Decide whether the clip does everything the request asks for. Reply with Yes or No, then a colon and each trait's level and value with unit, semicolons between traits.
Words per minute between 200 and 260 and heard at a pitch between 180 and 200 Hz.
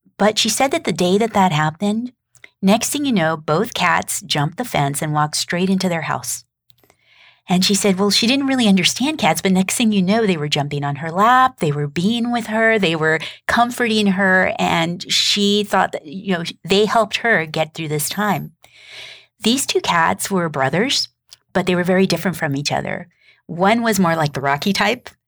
Yes: fast, 205 wpm; high, 190 Hz